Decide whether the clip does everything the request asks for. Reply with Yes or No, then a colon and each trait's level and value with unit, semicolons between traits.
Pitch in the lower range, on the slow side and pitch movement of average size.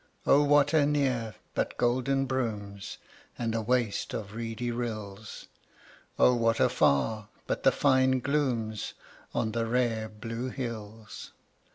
Yes: low, 115 Hz; slow, 125 wpm; average, 3.0 semitones